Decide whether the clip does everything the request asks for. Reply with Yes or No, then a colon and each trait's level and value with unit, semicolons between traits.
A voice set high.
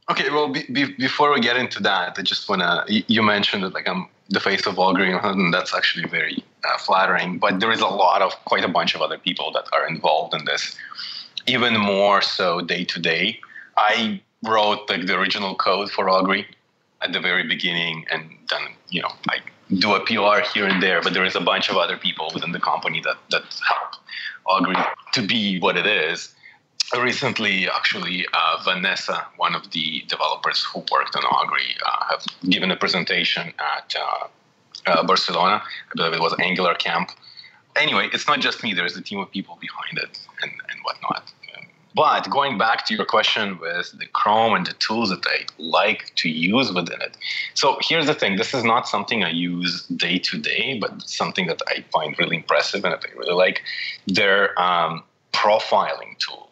No: low, 110 Hz